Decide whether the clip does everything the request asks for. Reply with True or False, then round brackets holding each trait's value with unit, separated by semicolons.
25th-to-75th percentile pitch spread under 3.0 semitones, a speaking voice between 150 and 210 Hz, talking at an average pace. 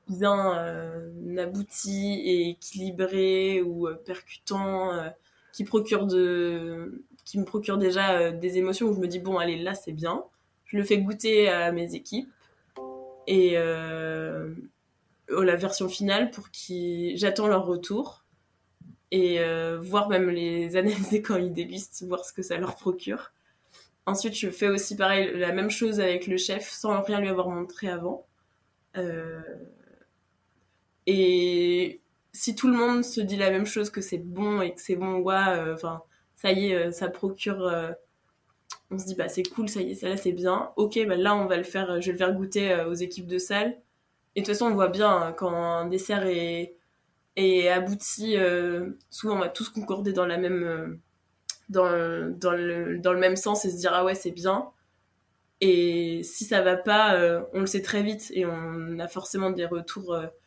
True (2.4 semitones; 185 Hz; 190 wpm)